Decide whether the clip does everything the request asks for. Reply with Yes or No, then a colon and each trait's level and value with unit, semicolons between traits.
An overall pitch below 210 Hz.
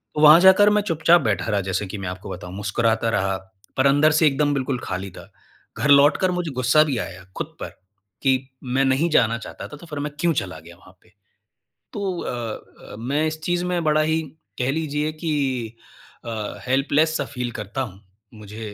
Yes: low, 135 Hz